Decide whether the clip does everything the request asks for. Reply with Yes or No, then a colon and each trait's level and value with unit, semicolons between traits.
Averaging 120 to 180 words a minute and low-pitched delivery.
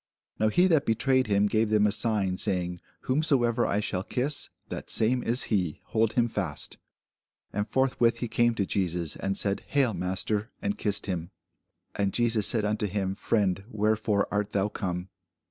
Yes: average, 170 wpm; low, 105 Hz